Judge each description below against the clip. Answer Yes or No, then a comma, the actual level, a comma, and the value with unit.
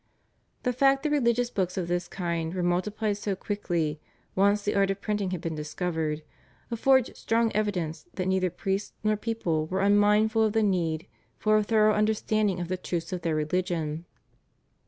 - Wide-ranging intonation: No, average, 3.6 semitones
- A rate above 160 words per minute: Yes, average, 175 wpm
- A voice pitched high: Yes, high, 195 Hz